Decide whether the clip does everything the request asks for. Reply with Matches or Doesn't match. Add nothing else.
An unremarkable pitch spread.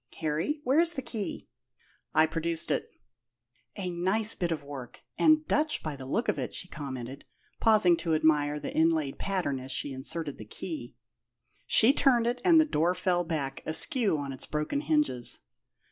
Doesn't match